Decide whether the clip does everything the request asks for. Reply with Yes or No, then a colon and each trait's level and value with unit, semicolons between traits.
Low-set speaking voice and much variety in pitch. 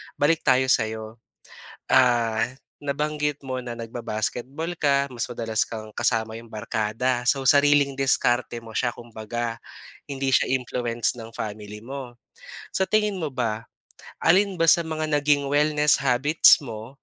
No: low, 125 Hz; average, 4.1 semitones